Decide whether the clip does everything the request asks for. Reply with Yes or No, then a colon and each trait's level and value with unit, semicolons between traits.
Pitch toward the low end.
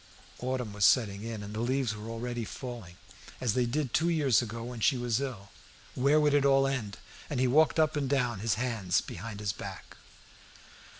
Yes: low, 120 Hz